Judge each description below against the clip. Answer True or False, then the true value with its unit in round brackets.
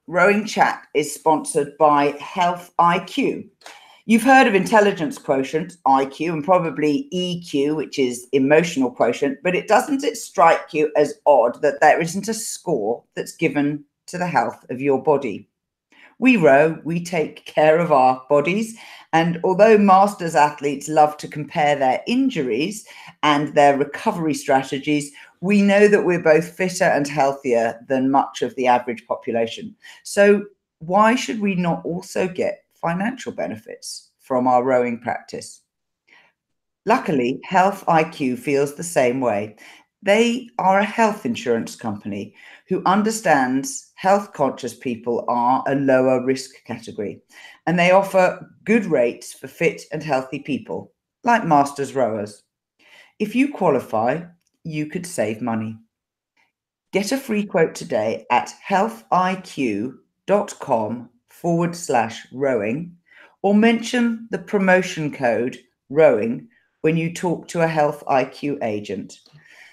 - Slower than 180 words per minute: True (135 wpm)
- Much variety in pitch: True (6.0 semitones)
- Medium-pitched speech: True (160 Hz)